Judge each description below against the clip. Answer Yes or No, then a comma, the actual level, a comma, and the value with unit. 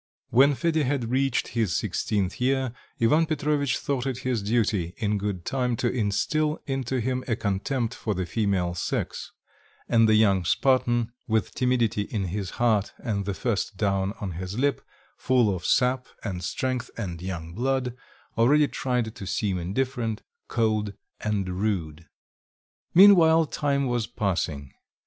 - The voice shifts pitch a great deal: No, average, 4.7 semitones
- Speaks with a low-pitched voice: Yes, low, 115 Hz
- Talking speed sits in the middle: Yes, average, 150 wpm